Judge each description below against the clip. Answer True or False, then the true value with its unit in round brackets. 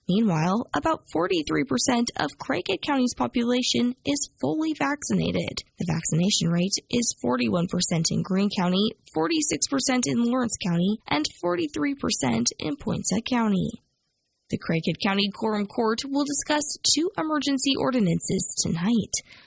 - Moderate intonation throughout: False (6.0 semitones)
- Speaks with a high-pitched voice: True (220 Hz)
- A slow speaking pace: True (115 wpm)